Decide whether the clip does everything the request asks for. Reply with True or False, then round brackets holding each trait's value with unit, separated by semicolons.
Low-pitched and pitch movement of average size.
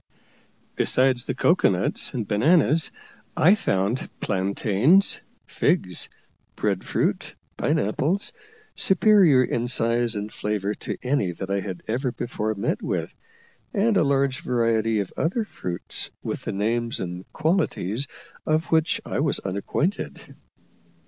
False (120 Hz; 7.4 semitones)